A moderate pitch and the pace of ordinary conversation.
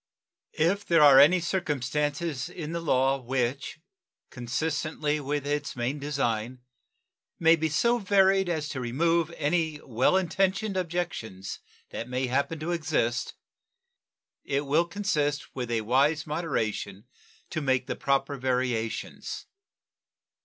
No: medium, 145 Hz; slow, 125 wpm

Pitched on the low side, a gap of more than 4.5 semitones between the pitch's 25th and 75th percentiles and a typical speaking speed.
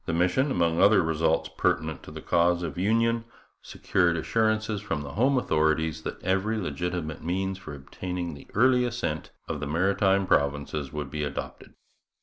Yes: very low, 90 Hz; average, 4.9 semitones; average, 160 wpm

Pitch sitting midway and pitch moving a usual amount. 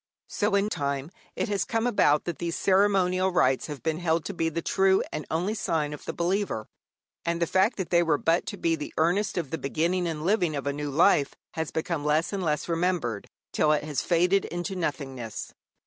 Yes: medium, 170 Hz; average, 3.8 semitones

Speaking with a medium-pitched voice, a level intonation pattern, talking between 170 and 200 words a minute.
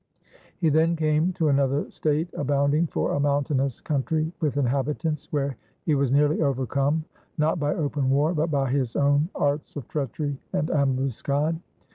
No: medium, 145 Hz; narrow, 1.9 semitones; average, 155 wpm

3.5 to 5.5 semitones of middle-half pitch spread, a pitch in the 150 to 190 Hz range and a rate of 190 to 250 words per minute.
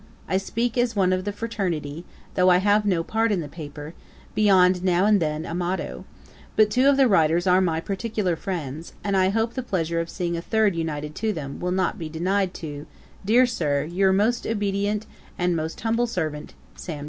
Yes: average, 4.1 semitones; medium, 185 Hz; average, 200 wpm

